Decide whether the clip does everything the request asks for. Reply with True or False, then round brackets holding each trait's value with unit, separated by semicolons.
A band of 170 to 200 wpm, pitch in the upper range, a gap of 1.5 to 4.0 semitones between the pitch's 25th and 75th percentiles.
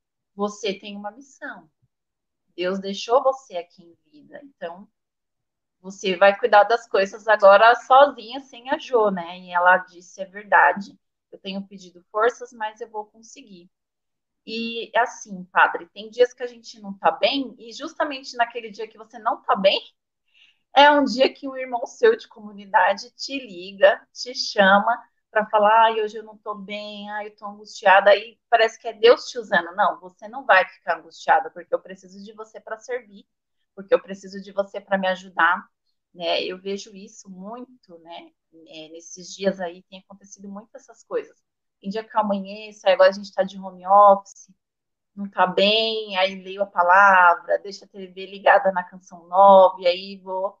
True (180 wpm; 205 Hz; 3.7 semitones)